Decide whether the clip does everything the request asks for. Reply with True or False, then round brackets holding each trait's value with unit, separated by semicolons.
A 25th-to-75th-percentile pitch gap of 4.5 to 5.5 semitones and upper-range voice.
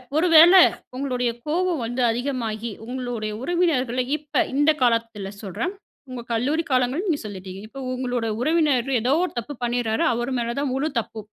False (4.1 semitones; 250 Hz)